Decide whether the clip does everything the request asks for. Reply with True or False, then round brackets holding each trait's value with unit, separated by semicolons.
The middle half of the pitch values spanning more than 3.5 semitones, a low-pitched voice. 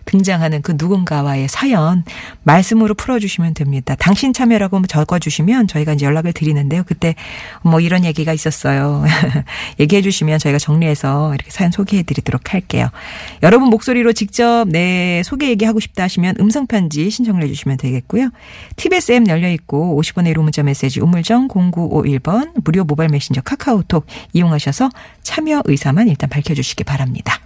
False (5.6 semitones; 170 Hz)